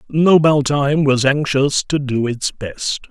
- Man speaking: Yes, male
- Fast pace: No, slow, 135 wpm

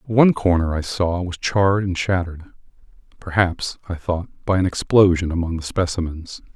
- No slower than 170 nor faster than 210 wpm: No, average, 155 wpm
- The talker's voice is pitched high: No, very low, 90 Hz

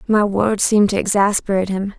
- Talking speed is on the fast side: No, average, 180 wpm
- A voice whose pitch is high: Yes, high, 200 Hz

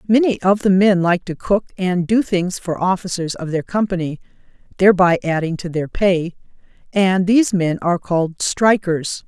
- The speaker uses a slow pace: No, average, 170 wpm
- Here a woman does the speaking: Yes, female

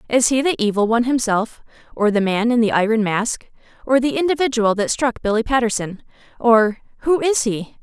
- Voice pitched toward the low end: No, high, 235 Hz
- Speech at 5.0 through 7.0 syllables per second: Yes, 5.4 syllables/s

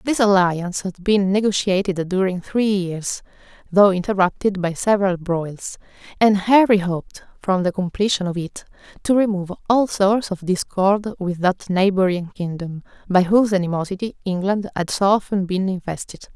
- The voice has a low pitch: No, high, 190 Hz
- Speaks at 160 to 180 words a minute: No, average, 145 wpm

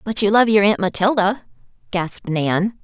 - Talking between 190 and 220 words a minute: No, average, 170 wpm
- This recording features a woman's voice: Yes, female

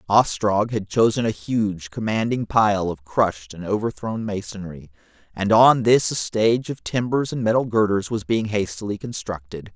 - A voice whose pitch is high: No, low, 105 Hz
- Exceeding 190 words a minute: No, average, 160 wpm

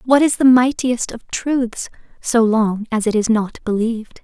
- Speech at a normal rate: Yes, average, 185 wpm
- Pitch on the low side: No, high, 235 Hz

